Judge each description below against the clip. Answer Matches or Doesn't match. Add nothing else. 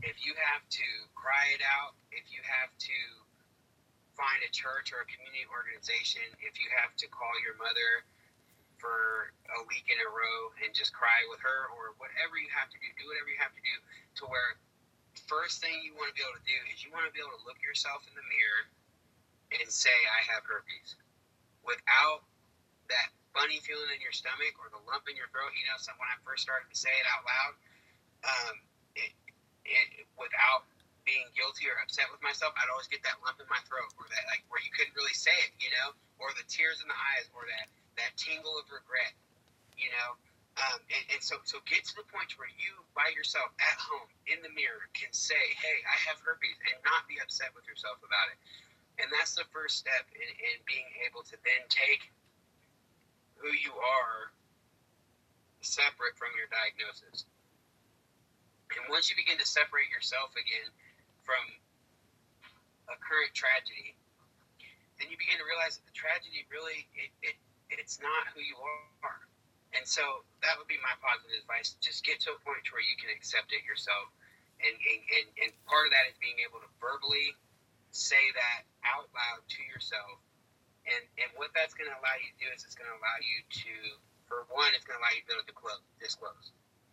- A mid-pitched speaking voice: Matches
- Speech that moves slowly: Doesn't match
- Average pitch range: Doesn't match